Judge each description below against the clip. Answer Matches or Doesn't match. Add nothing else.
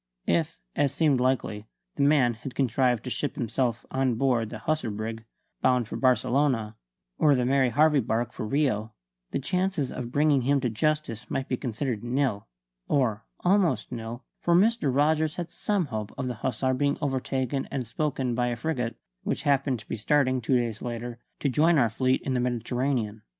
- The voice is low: Matches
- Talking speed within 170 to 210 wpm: Matches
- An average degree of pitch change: Matches